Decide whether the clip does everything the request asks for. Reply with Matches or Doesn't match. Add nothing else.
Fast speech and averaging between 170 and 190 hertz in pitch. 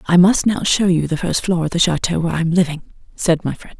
Matches